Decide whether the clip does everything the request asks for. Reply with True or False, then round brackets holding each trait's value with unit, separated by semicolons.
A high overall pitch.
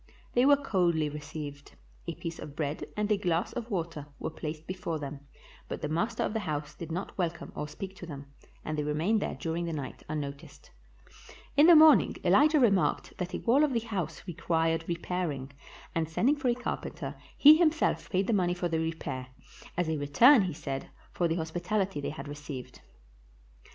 False (170 Hz)